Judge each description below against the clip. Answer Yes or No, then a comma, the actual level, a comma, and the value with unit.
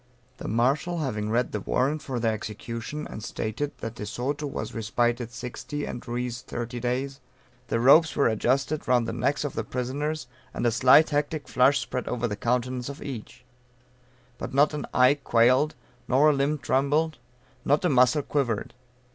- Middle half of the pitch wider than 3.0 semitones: Yes, average, 3.4 semitones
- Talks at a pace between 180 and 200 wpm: No, average, 170 wpm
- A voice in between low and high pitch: No, low, 125 Hz